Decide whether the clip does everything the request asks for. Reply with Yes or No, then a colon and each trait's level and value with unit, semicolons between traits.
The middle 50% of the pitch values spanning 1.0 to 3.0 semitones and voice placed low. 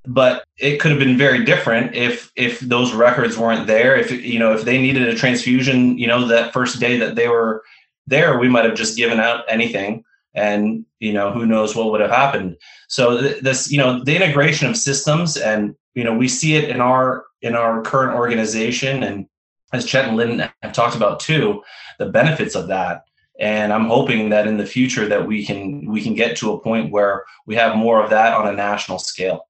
Yes: narrow, 2.5 semitones; low, 120 Hz